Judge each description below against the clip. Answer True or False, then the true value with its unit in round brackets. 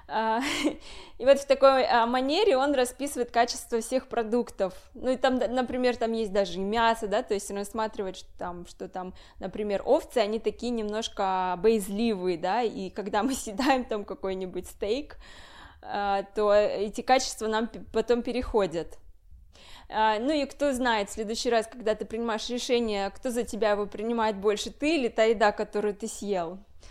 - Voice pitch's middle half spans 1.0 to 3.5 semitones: True (3.1 semitones)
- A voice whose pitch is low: False (220 Hz)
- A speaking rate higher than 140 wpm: True (160 wpm)